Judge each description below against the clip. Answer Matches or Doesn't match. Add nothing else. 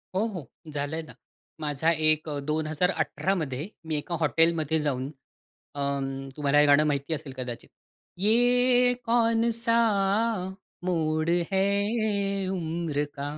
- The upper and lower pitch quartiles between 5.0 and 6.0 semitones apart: Matches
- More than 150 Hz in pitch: Matches